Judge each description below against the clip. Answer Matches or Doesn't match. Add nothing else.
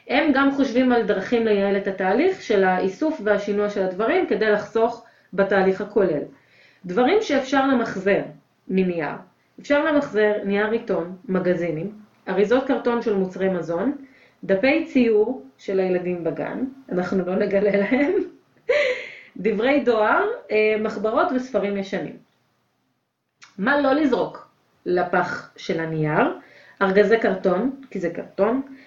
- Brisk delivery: Doesn't match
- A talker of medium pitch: Doesn't match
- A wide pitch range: Matches